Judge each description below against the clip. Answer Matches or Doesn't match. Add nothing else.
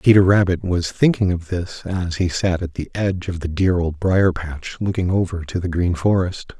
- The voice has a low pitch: Matches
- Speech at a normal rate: Doesn't match